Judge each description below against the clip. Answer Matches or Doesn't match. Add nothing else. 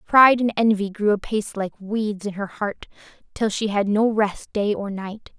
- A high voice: Matches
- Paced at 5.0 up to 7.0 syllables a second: Doesn't match